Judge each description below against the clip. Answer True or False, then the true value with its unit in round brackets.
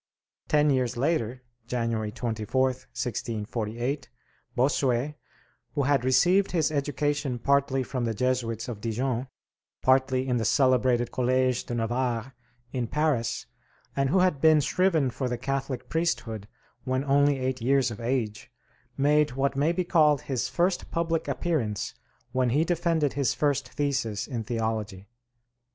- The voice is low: True (130 Hz)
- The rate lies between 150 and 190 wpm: False (140 wpm)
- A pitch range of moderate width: True (3.4 semitones)